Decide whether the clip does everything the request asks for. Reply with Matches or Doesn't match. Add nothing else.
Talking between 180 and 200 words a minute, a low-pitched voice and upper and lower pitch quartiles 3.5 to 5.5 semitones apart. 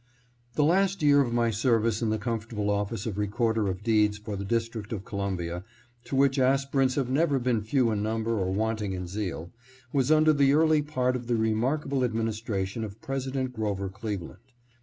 Matches